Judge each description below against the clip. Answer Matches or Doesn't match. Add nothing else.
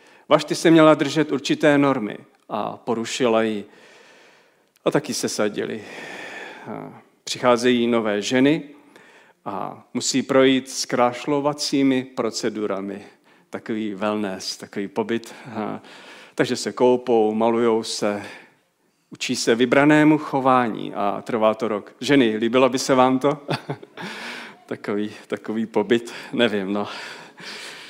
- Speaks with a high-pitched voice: Doesn't match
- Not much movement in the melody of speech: Doesn't match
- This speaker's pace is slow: Matches